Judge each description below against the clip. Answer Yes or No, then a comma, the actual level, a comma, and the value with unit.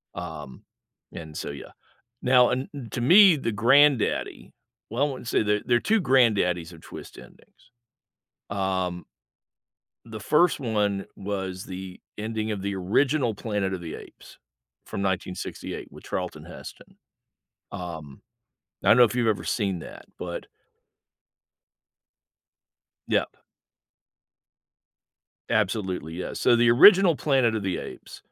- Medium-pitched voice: No, low, 105 Hz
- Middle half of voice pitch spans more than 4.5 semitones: Yes, average, 5.1 semitones